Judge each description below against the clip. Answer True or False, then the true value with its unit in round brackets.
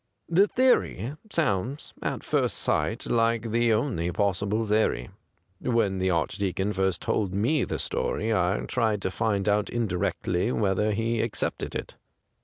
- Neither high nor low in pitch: False (105 Hz)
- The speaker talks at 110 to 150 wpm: True (140 wpm)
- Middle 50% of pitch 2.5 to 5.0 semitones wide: True (3.3 semitones)